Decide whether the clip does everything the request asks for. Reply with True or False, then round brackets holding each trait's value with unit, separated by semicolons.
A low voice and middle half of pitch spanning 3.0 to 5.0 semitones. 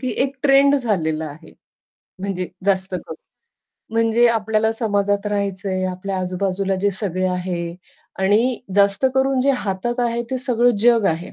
False (200 Hz; 4.3 semitones)